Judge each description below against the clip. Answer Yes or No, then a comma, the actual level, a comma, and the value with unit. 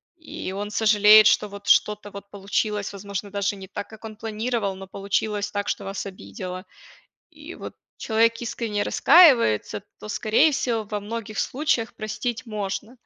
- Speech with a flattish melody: Yes, narrow, 2.0 semitones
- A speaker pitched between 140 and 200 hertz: No, high, 210 Hz